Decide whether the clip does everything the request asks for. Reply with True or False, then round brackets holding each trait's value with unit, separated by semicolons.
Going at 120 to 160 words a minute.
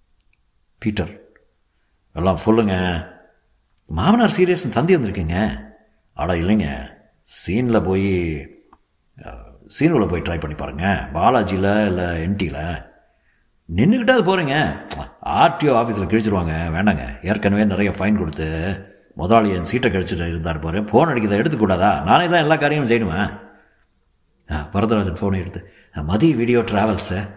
False (110 wpm)